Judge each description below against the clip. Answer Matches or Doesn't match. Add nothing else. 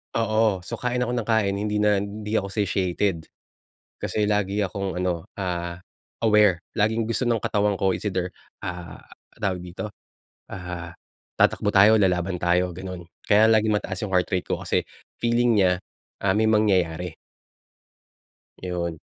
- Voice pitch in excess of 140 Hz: Doesn't match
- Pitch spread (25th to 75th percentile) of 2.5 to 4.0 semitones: Matches